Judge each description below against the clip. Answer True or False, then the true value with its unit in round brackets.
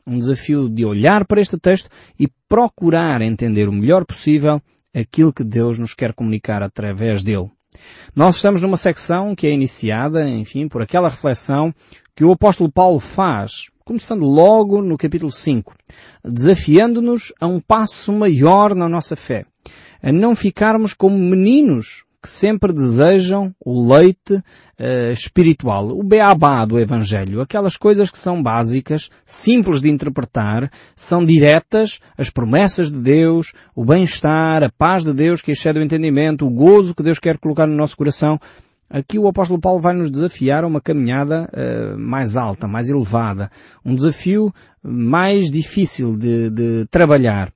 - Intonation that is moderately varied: False (6.9 semitones)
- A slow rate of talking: False (150 wpm)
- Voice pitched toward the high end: False (155 Hz)